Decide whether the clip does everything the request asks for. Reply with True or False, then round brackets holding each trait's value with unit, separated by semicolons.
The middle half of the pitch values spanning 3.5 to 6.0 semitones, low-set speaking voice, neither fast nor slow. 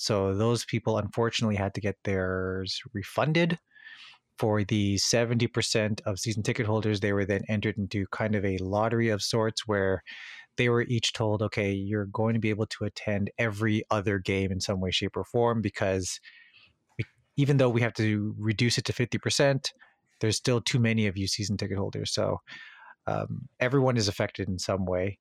False (2.7 semitones; 110 Hz; 180 wpm)